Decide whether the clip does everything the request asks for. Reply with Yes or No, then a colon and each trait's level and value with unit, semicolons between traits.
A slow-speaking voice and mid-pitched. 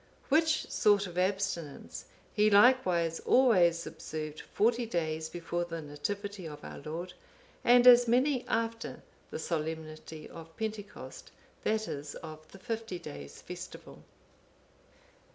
Yes: slow, 120 wpm; medium, 180 Hz